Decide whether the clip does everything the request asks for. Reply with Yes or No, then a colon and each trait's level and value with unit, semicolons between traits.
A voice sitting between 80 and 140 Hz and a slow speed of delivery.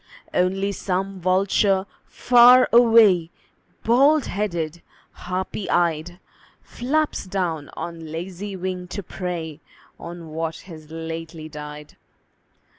No: medium, 180 Hz; slow, 100 wpm